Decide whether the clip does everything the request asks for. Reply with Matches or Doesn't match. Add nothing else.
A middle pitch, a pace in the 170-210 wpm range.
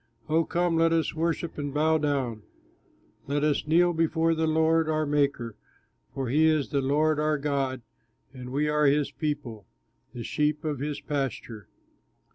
Doesn't match